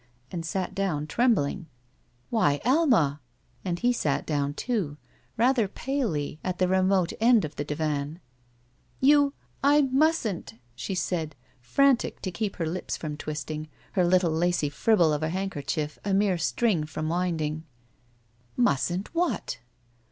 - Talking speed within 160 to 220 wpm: No, average, 145 wpm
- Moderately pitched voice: Yes, medium, 180 Hz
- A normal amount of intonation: No, wide, 6.6 semitones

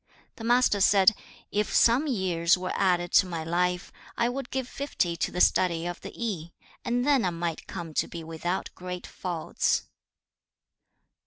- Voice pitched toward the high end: No, medium, 180 Hz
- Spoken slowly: No, average, 165 wpm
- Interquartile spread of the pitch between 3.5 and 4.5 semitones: No, average, 5.2 semitones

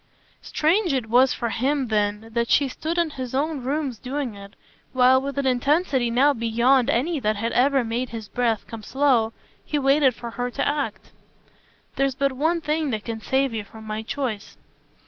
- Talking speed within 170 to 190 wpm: Yes, average, 185 wpm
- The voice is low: No, very high, 255 Hz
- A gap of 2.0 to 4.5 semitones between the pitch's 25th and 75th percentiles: Yes, average, 3.6 semitones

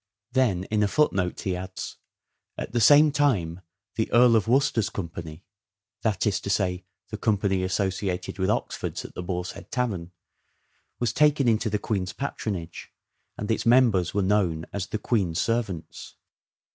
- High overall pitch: No, low, 100 Hz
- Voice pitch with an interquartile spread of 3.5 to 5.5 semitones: Yes, average, 4.3 semitones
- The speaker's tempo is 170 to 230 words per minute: No, average, 160 wpm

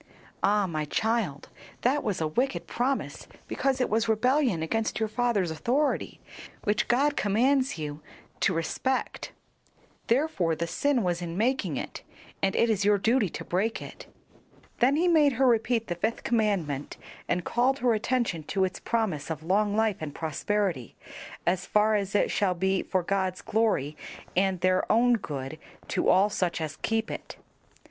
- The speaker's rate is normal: Yes, average, 165 wpm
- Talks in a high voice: Yes, high, 210 Hz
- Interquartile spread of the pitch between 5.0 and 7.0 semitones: Yes, wide, 5.5 semitones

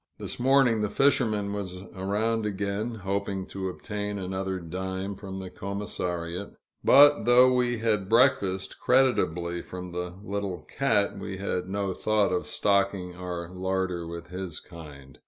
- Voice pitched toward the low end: Yes, very low, 95 Hz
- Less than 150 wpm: Yes, average, 140 wpm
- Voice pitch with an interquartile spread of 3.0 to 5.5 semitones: No, narrow, 2.5 semitones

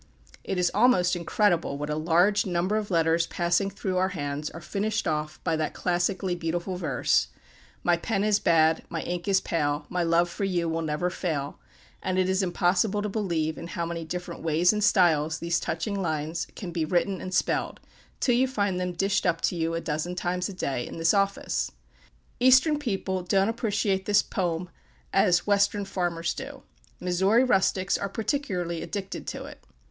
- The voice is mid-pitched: Yes, medium, 180 Hz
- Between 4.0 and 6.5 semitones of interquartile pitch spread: No, average, 3.1 semitones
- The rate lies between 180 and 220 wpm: Yes, average, 185 wpm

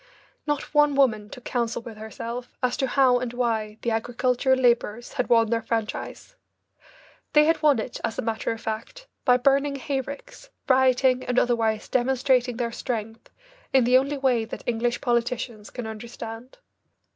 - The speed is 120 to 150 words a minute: No, average, 165 wpm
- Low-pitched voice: No, high, 245 Hz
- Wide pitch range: No, narrow, 2.5 semitones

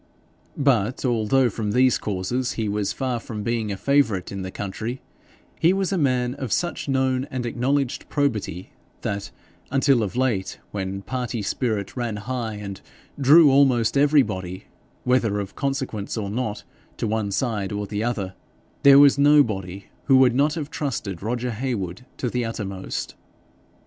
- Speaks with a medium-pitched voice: No, low, 120 Hz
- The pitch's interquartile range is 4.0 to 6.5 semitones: Yes, average, 4.5 semitones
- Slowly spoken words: No, average, 155 wpm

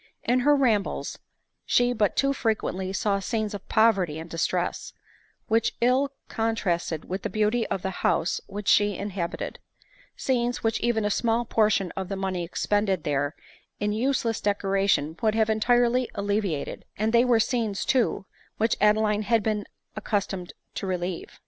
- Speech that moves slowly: No, average, 155 wpm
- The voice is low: No, high, 210 Hz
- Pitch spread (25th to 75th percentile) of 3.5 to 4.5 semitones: No, average, 3.0 semitones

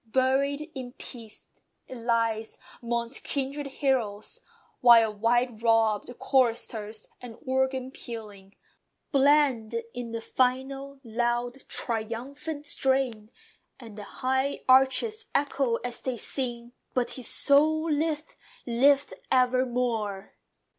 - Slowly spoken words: Yes, slow, 105 wpm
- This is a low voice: No, very high, 250 Hz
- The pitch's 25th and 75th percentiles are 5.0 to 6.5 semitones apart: No, average, 2.9 semitones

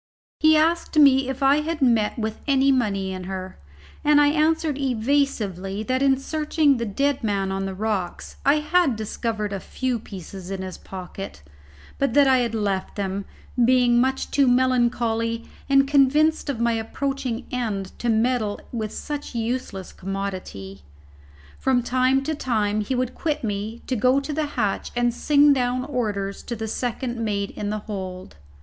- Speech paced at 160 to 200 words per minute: Yes, average, 170 wpm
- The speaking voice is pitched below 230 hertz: No, high, 240 Hz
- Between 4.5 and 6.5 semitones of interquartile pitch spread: Yes, average, 4.9 semitones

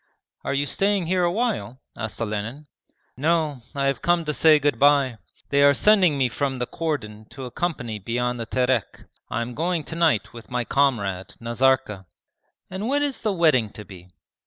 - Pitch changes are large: Yes, wide, 5.9 semitones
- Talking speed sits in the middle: Yes, average, 185 wpm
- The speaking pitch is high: No, low, 135 Hz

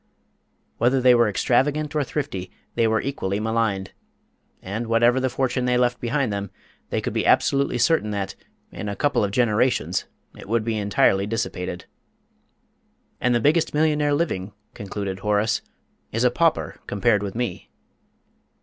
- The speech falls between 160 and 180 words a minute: No, average, 150 wpm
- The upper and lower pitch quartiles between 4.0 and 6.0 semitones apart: Yes, average, 4.3 semitones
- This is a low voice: Yes, low, 115 Hz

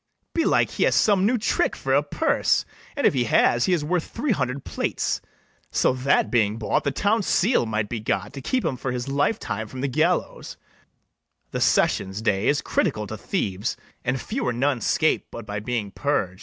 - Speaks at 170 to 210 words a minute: Yes, average, 200 wpm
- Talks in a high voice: No, low, 130 Hz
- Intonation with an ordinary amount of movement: No, wide, 7.4 semitones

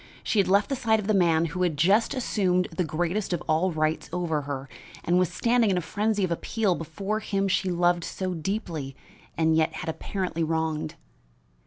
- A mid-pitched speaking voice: Yes, medium, 180 Hz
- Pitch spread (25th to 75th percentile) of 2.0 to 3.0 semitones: No, average, 3.7 semitones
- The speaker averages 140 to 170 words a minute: No, average, 195 wpm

